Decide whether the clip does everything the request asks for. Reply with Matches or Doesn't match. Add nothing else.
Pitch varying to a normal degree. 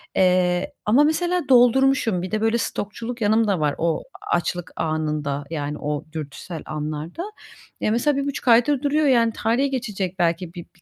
Doesn't match